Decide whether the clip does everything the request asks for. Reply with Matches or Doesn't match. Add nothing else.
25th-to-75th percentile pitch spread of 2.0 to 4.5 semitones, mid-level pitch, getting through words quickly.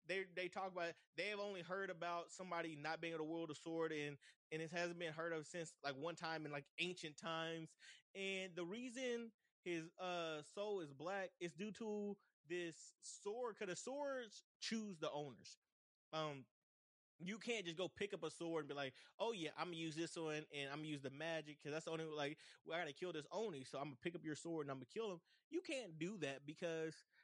Matches